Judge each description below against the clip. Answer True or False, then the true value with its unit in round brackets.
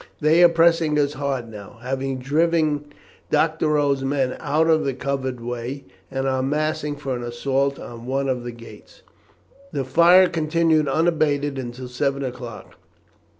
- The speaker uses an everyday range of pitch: True (3.0 semitones)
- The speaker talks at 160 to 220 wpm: False (150 wpm)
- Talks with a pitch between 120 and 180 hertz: True (140 Hz)